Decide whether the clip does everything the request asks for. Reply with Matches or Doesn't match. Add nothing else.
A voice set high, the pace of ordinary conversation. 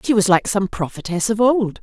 Doesn't match